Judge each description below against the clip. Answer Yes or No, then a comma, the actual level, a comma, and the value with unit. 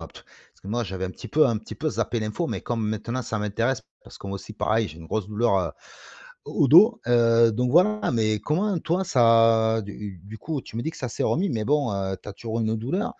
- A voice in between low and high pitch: No, low, 115 Hz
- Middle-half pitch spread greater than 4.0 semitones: Yes, average, 4.6 semitones